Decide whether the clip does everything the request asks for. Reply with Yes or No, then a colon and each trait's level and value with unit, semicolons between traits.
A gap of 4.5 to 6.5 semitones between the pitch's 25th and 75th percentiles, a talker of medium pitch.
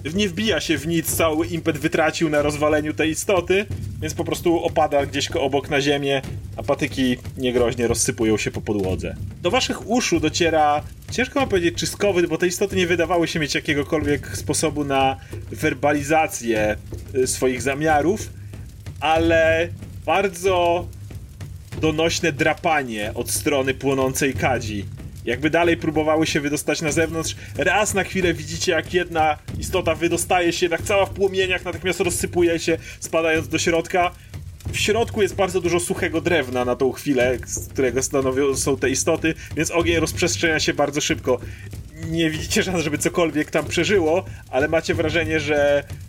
Yes: average, 5.1 semitones; medium, 155 Hz